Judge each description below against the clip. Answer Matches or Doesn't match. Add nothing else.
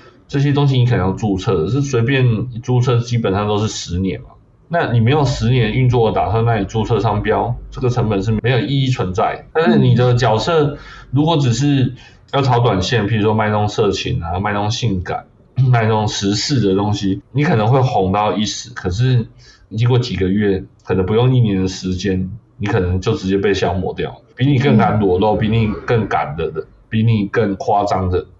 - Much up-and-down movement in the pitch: Doesn't match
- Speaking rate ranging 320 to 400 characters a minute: Doesn't match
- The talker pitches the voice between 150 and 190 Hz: Doesn't match